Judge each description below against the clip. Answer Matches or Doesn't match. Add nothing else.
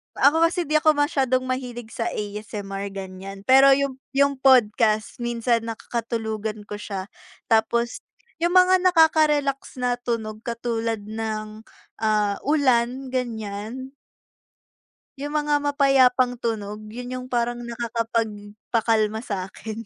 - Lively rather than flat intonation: Doesn't match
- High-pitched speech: Matches